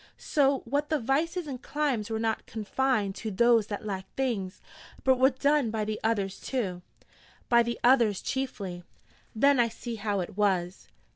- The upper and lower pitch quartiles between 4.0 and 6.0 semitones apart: Yes, average, 4.5 semitones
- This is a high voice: Yes, high, 230 Hz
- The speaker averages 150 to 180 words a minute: Yes, average, 165 wpm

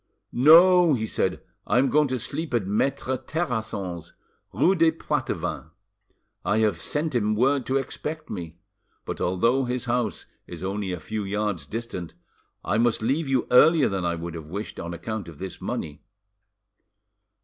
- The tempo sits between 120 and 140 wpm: No, average, 160 wpm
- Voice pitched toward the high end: No, low, 115 Hz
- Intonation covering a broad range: Yes, wide, 6.4 semitones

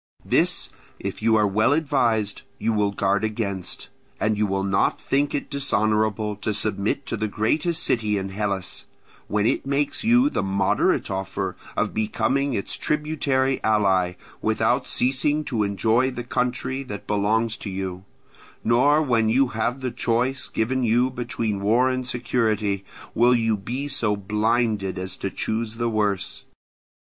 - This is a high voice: No, low, 110 Hz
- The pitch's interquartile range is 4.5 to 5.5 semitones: No, average, 3.8 semitones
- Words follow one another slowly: No, average, 155 wpm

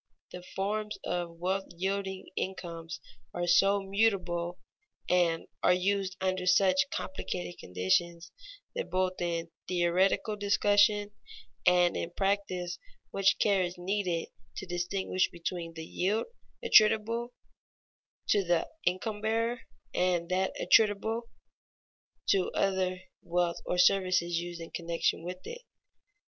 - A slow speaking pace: Yes, slow, 120 wpm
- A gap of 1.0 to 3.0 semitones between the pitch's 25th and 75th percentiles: Yes, narrow, 2.4 semitones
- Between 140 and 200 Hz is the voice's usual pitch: Yes, medium, 185 Hz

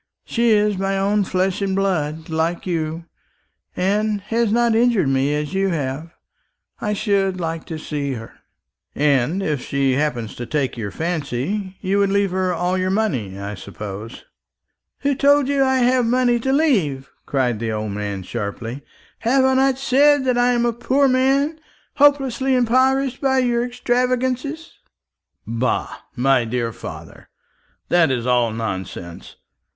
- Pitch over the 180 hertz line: Yes, high, 190 Hz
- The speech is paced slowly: No, average, 155 wpm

